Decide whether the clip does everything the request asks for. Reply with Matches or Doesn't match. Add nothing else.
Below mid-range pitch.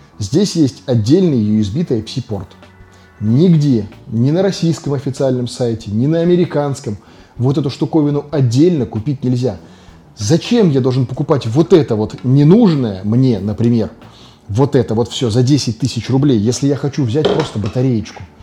Matches